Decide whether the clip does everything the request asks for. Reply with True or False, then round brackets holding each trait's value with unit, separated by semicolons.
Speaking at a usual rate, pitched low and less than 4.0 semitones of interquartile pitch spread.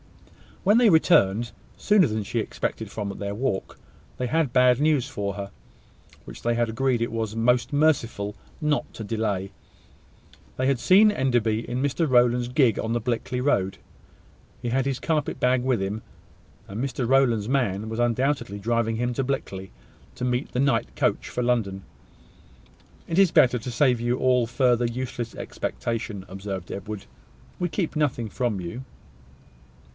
True (160 wpm; 120 Hz; 3.4 semitones)